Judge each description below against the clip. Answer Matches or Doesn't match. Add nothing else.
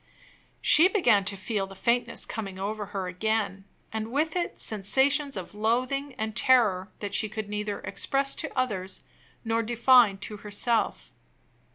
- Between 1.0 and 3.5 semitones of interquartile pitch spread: Doesn't match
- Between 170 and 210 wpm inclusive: Doesn't match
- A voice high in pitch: Matches